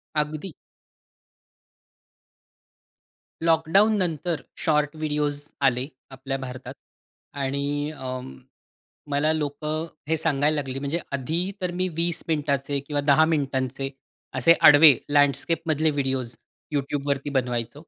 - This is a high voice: No, medium, 145 Hz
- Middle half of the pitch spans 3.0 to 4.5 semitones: No, narrow, 2.6 semitones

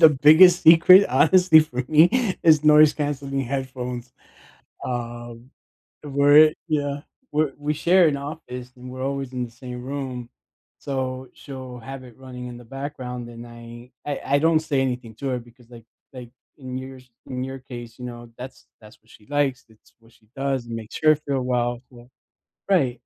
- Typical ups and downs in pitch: Yes, average, 3.0 semitones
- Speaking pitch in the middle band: No, low, 130 Hz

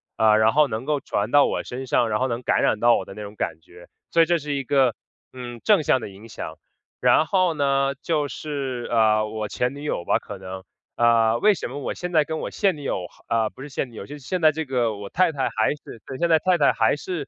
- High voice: No, low, 130 Hz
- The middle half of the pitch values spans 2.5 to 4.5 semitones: No, average, 5.2 semitones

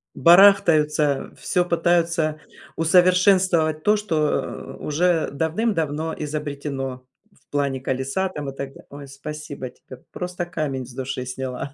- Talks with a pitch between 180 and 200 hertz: No, medium, 155 Hz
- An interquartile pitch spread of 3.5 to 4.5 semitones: Yes, average, 4.1 semitones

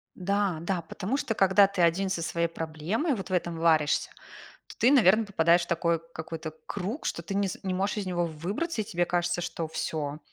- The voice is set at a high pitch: No, medium, 175 Hz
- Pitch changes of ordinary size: Yes, average, 3.1 semitones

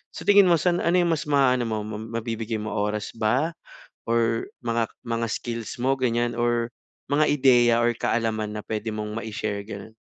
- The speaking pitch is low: Yes, low, 115 Hz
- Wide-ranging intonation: No, average, 2.8 semitones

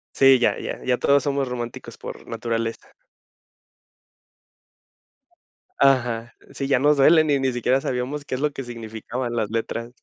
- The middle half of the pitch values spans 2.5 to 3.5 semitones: Yes, average, 2.8 semitones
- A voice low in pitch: Yes, low, 125 Hz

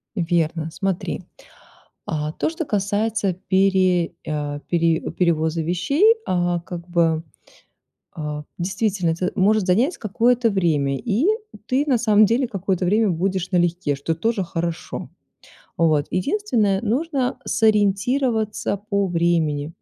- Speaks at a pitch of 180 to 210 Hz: Yes, medium, 185 Hz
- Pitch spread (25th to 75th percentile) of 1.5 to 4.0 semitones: No, average, 4.6 semitones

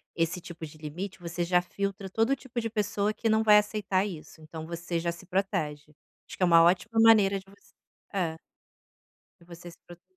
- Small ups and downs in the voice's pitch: No, average, 3.4 semitones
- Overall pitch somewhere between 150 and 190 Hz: Yes, medium, 185 Hz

